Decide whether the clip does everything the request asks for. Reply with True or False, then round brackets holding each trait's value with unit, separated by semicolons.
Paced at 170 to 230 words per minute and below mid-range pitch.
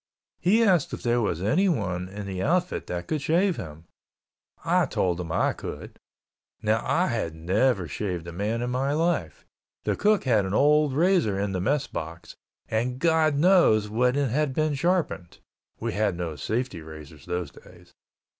True (175 wpm; 115 Hz)